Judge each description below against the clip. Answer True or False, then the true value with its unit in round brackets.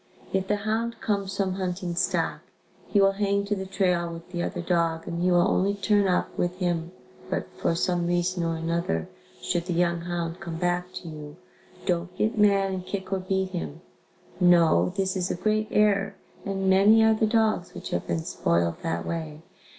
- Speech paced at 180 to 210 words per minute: True (195 wpm)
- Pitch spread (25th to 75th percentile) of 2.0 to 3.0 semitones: True (2.6 semitones)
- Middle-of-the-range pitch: True (180 Hz)